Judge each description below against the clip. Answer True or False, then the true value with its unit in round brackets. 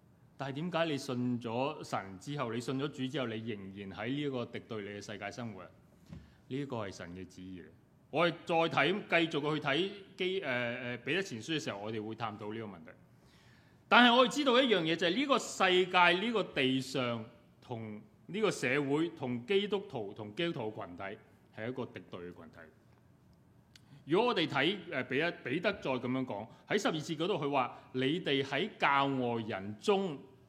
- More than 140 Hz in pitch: False (130 Hz)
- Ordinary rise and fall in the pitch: False (6.5 semitones)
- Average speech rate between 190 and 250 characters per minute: False (275 characters per minute)